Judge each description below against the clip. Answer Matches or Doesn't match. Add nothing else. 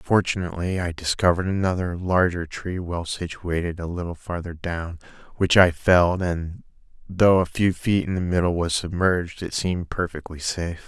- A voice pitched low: Matches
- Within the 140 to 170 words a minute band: Matches